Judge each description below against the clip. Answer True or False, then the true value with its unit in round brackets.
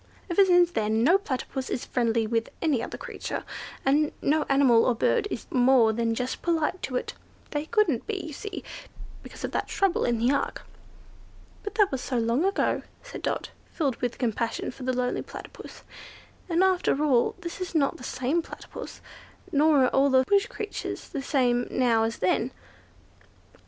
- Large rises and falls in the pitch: True (5.8 semitones)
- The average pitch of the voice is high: True (270 Hz)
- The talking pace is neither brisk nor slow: True (175 wpm)